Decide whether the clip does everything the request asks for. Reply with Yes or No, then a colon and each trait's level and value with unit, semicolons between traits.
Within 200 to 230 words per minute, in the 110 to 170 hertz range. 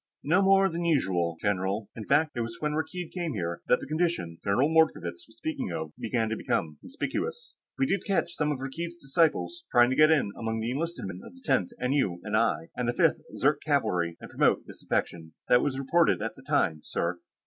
Yes: fast, 205 wpm; low, 135 Hz